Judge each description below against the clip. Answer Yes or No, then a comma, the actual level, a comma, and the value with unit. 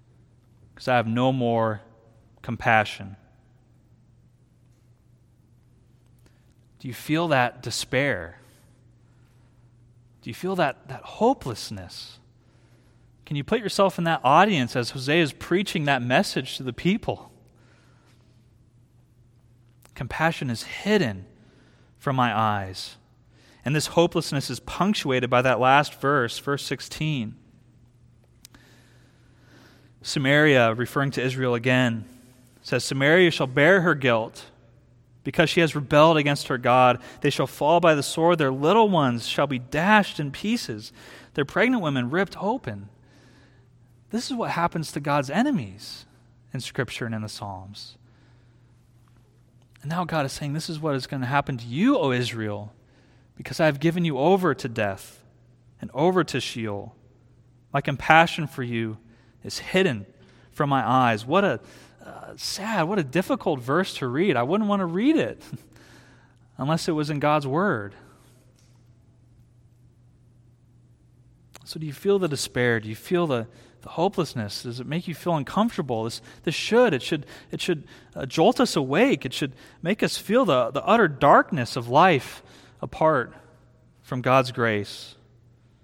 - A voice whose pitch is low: Yes, low, 125 Hz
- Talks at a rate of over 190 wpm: No, average, 140 wpm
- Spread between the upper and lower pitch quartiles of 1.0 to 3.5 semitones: No, average, 4.1 semitones